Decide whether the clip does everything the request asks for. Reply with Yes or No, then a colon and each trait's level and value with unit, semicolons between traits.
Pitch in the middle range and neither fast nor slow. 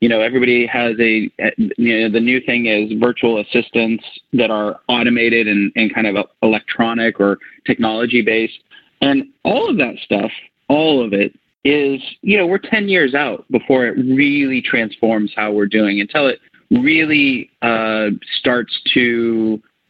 No: low, 115 Hz; average, 155 wpm